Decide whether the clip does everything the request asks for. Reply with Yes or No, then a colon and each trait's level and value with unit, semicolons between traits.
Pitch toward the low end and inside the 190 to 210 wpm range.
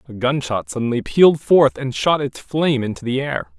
Yes: low, 130 Hz; average, 200 wpm